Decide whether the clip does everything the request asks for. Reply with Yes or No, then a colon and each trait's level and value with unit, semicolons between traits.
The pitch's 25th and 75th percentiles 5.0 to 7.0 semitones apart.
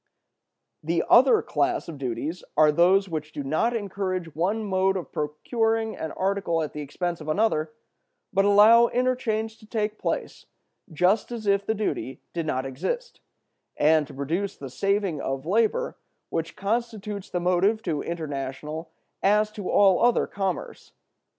Yes: wide, 5.5 semitones